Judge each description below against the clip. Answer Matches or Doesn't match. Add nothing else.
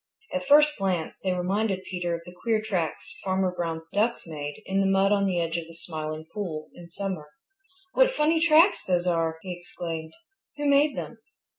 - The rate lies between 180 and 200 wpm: Matches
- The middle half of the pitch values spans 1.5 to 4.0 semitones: Doesn't match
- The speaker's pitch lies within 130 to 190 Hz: Matches